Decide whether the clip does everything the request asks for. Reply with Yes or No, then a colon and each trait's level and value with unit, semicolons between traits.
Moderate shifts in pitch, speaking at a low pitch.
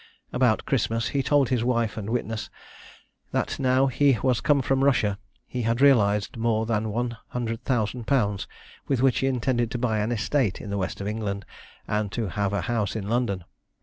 Yes: average, 3.3 semitones; low, 115 Hz